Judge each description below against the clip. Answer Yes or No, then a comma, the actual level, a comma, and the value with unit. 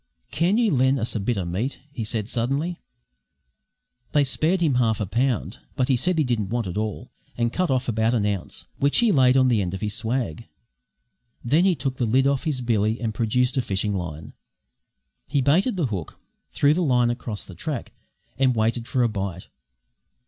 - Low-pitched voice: Yes, low, 120 Hz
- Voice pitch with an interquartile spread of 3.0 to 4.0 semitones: No, average, 4.4 semitones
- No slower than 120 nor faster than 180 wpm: No, average, 200 wpm